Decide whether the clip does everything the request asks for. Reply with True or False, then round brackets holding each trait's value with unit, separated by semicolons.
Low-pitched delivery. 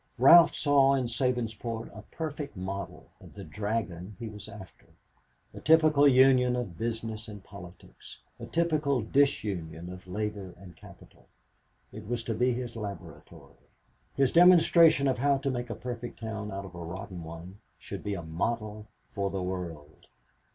True (110 Hz)